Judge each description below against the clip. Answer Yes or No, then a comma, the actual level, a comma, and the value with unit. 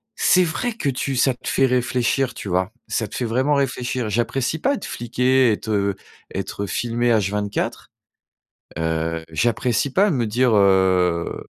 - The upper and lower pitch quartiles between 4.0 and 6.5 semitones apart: Yes, average, 4.6 semitones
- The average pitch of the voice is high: No, low, 120 Hz